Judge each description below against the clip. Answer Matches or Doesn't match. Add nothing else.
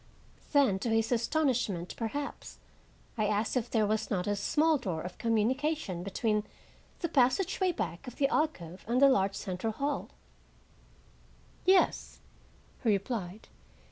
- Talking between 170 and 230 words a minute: Doesn't match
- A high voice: Matches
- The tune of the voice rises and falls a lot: Matches